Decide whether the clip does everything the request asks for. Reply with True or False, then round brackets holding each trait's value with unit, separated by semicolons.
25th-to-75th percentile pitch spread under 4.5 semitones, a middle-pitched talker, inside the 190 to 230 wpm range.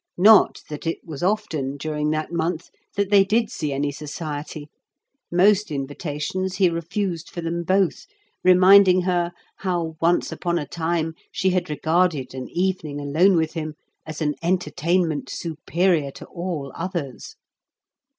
False (3.3 semitones; 170 Hz; 140 wpm)